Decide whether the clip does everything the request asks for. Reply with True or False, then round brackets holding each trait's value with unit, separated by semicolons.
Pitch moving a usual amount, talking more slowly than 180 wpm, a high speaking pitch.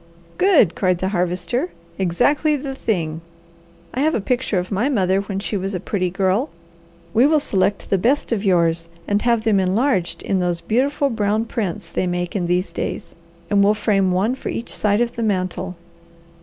False (4.4 semitones; 185 wpm; 200 Hz)